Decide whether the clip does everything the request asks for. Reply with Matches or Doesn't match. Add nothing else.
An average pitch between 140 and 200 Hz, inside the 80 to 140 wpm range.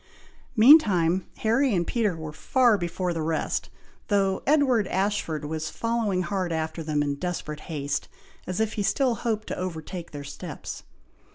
Doesn't match